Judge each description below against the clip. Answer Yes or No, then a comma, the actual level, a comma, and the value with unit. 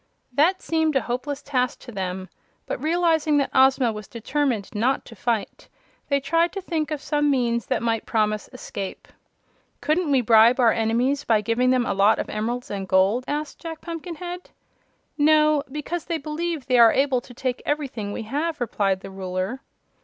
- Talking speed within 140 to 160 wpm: No, average, 175 wpm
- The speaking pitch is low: No, very high, 255 Hz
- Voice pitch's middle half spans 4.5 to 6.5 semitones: Yes, average, 5.2 semitones